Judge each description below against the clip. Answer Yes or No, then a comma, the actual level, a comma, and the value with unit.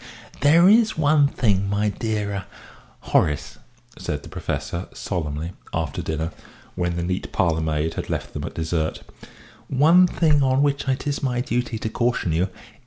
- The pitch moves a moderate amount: No, wide, 8.9 semitones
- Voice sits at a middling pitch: No, low, 105 Hz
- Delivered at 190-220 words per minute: No, average, 165 wpm